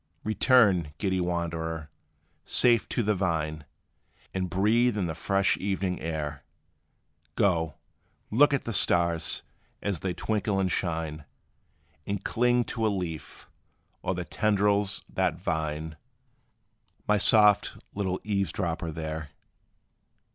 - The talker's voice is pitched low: Yes, very low, 95 Hz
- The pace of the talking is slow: Yes, slow, 115 wpm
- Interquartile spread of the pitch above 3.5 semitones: Yes, average, 4.1 semitones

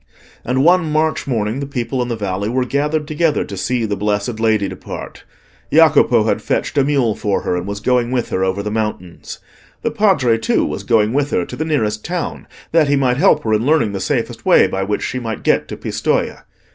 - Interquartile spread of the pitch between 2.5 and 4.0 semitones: No, wide, 5.6 semitones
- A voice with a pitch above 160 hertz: No, low, 120 Hz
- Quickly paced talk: Yes, fast, 220 wpm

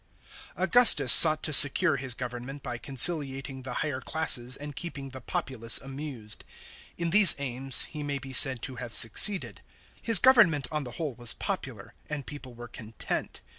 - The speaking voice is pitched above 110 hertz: Yes, low, 135 Hz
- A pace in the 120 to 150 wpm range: No, average, 170 wpm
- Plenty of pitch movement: No, average, 3.5 semitones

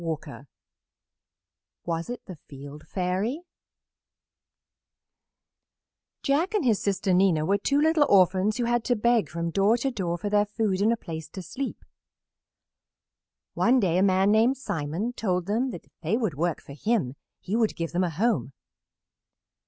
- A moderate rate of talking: Yes, average, 150 wpm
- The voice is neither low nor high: No, high, 195 Hz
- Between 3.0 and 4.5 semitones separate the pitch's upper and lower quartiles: No, wide, 5.6 semitones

